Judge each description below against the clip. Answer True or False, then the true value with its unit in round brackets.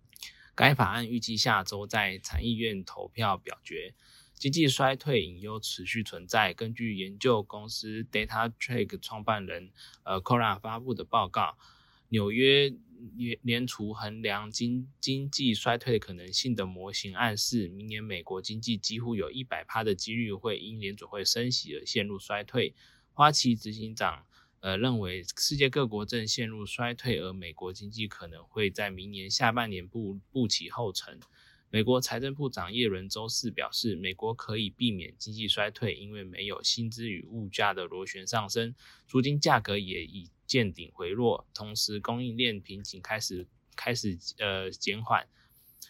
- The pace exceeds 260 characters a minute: False (255 characters per minute)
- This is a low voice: True (110 Hz)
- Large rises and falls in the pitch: False (3.2 semitones)